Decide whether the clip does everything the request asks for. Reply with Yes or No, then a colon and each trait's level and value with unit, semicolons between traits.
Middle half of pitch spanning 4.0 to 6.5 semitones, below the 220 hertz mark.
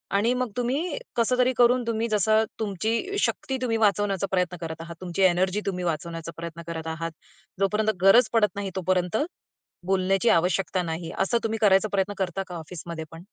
Yes: average, 4.4 semitones; high, 195 Hz